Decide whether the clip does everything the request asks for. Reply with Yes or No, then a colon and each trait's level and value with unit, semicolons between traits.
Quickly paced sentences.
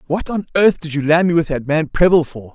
Yes: fast, 285 wpm